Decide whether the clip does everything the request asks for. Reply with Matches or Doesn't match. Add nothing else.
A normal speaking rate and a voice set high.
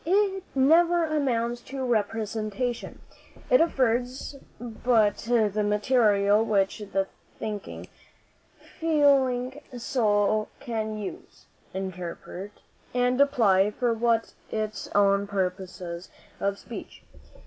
Doesn't match